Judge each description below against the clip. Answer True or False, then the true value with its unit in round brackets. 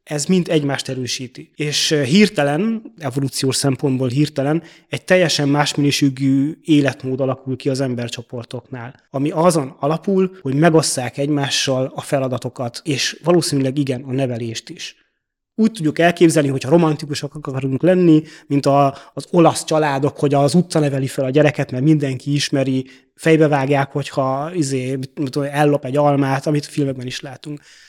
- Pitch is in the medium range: True (145 Hz)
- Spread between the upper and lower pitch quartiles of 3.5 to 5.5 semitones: False (2.7 semitones)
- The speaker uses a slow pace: False (140 wpm)